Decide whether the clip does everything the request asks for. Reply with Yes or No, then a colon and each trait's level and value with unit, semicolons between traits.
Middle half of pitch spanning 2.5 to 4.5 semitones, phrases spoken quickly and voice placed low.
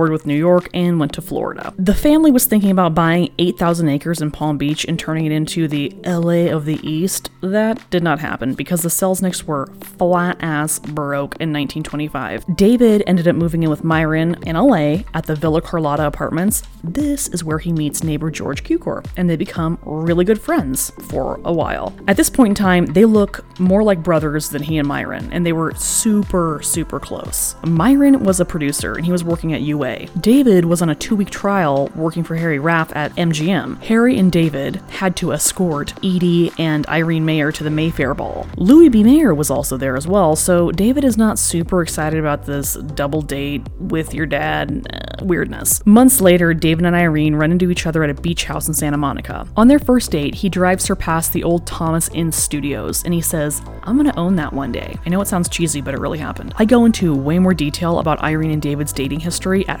No: average, 3.5 semitones; fast, 210 wpm; medium, 165 Hz